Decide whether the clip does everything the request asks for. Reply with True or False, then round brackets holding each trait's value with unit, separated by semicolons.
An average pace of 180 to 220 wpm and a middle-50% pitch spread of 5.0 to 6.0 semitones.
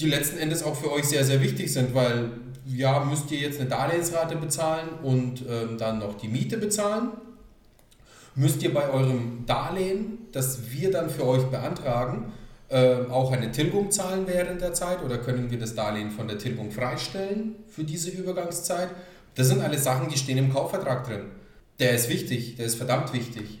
True (185 wpm; 5.6 semitones)